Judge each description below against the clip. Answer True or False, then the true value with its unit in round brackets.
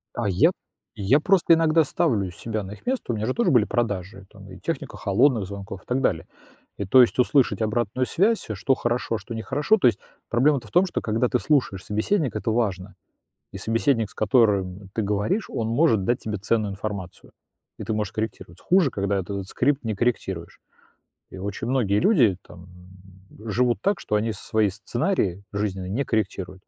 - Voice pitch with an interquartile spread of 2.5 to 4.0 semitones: False (4.5 semitones)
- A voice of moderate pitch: False (110 Hz)